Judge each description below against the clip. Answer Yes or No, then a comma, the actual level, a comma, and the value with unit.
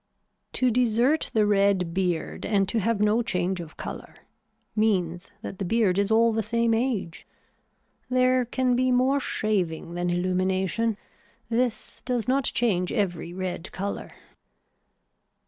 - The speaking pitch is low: No, high, 210 Hz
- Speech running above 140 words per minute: No, slow, 135 wpm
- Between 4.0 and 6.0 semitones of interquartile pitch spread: Yes, average, 4.4 semitones